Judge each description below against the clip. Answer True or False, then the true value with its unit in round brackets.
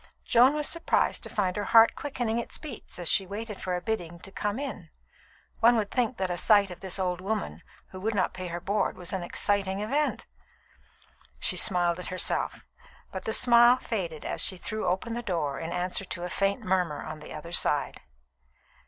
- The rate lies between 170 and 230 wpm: True (200 wpm)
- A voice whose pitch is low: False (195 Hz)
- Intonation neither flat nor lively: True (4.0 semitones)